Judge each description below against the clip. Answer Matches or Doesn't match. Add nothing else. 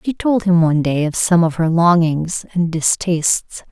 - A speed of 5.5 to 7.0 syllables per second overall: Doesn't match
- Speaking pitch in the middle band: Matches